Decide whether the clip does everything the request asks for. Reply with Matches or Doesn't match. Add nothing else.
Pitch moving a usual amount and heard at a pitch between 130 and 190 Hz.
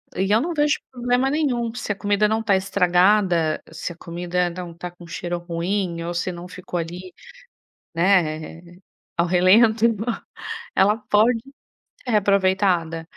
Matches